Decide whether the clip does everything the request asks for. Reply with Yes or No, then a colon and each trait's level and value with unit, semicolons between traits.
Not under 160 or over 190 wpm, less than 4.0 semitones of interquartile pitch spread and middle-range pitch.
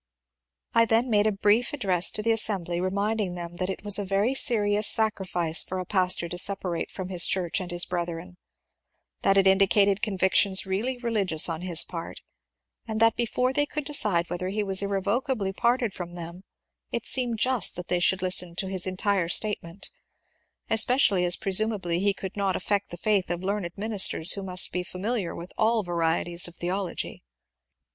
No: average, 180 wpm; average, 3.2 semitones; high, 195 Hz